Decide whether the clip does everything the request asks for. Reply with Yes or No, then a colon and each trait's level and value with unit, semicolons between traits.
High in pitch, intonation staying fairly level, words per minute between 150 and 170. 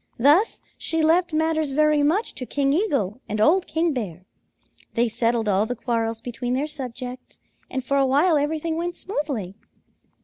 No: very high, 275 Hz; average, 5.1 semitones; average, 165 wpm